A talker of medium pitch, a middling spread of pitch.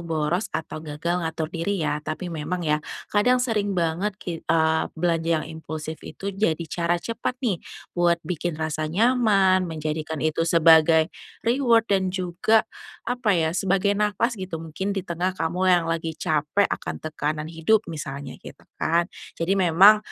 Yes: medium, 170 Hz; average, 3.6 semitones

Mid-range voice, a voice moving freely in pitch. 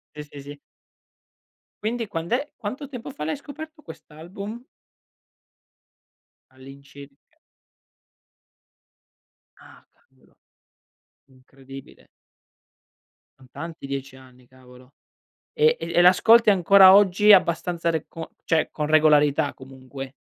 Yes: medium, 160 Hz; wide, 7.0 semitones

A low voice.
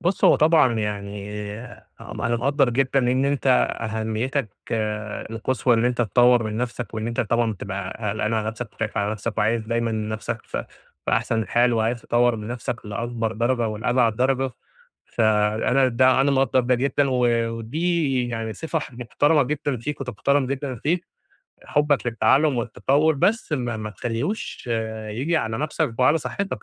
Yes: low, 120 Hz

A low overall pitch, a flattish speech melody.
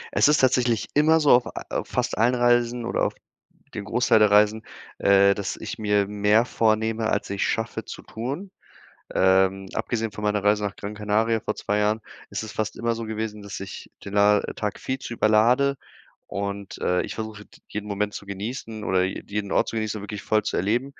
Yes: low, 105 Hz; narrow, 2.1 semitones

